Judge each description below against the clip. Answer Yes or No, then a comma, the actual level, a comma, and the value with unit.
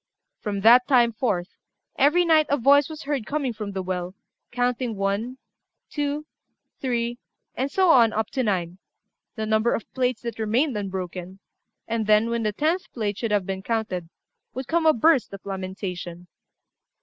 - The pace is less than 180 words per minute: Yes, average, 170 wpm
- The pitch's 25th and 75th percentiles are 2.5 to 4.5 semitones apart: No, average, 5.1 semitones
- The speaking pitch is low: No, high, 230 Hz